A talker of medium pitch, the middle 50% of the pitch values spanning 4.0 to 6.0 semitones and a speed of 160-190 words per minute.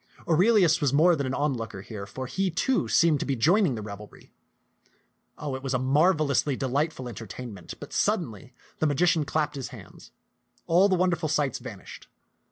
Yes: medium, 145 Hz; average, 4.7 semitones; average, 175 wpm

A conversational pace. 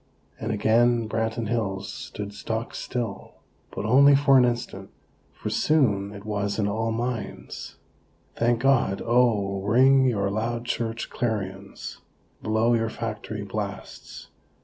No: slow, 125 wpm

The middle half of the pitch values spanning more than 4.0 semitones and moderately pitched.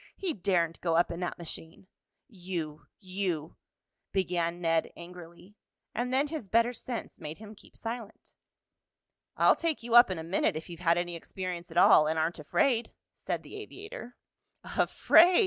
Yes: wide, 5.5 semitones; medium, 180 Hz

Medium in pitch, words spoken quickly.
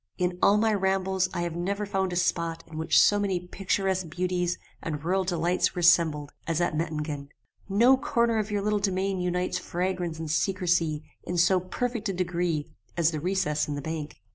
No: medium, 180 Hz; average, 185 wpm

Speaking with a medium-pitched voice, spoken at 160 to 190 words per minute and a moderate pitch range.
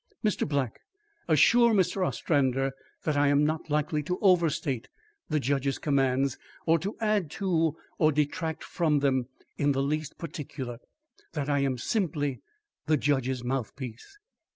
No: medium, 145 Hz; average, 140 wpm; average, 3.3 semitones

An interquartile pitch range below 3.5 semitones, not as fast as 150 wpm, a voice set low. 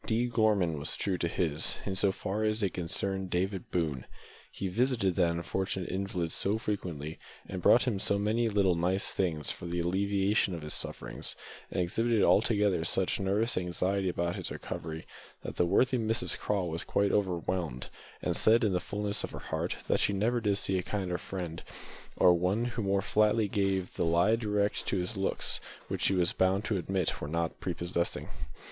No: average, 3.0 semitones; average, 185 wpm; very low, 95 Hz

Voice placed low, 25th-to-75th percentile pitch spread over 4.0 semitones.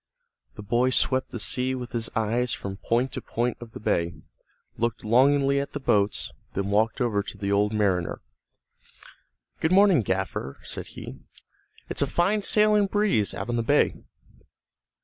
Yes: low, 120 Hz; average, 4.9 semitones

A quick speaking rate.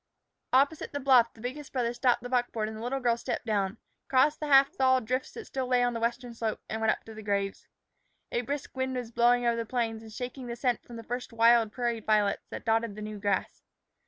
Yes: fast, 240 wpm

